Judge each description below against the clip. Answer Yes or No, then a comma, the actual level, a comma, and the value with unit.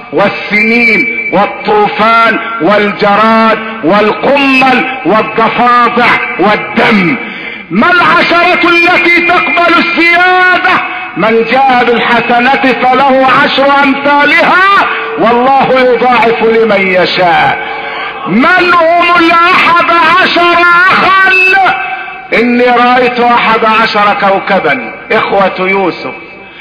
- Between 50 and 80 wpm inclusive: Yes, average, 75 wpm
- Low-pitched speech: No, very high, 255 Hz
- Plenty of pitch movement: Yes, wide, 7.6 semitones